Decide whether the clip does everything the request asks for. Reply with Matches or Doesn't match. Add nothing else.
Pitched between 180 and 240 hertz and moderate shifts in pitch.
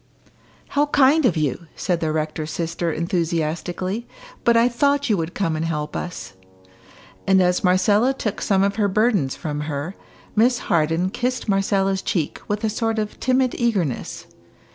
Doesn't match